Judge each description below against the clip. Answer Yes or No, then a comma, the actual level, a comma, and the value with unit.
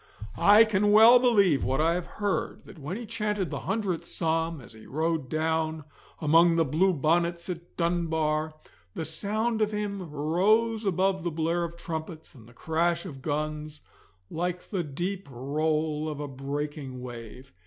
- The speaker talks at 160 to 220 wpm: Yes, average, 165 wpm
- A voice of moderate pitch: Yes, medium, 165 Hz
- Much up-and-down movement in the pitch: No, average, 3.8 semitones